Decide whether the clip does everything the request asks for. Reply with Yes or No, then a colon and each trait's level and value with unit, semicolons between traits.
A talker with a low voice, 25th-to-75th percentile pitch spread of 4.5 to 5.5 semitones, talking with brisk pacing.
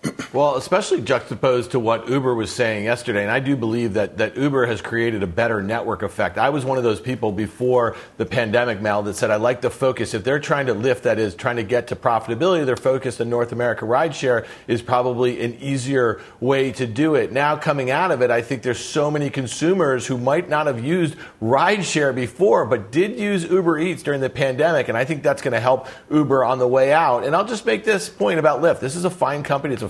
No: low, 130 Hz; average, 3.6 semitones; fast, 235 wpm